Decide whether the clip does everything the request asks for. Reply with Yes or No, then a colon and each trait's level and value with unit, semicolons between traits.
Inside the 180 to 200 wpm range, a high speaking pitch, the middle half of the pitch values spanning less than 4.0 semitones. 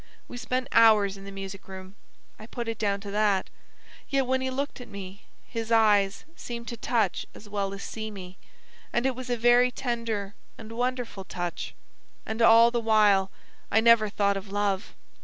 Yes: average, 185 wpm; high, 220 Hz; average, 3.1 semitones